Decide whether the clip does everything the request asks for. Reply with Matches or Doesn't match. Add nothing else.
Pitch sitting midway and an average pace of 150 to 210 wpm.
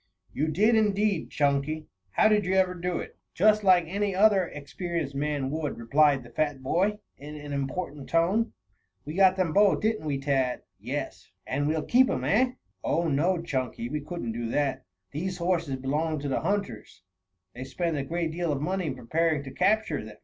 Matches